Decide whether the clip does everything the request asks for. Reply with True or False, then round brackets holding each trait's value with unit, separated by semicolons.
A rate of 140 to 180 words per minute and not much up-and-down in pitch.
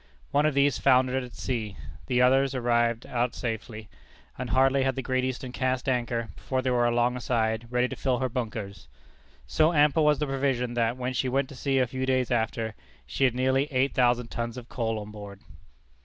False (200 wpm; 2.0 semitones)